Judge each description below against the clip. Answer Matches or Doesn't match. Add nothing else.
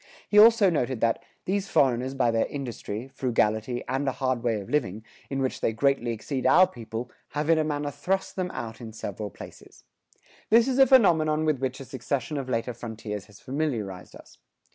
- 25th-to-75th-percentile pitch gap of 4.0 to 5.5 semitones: Matches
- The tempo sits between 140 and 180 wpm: Doesn't match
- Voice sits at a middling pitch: Doesn't match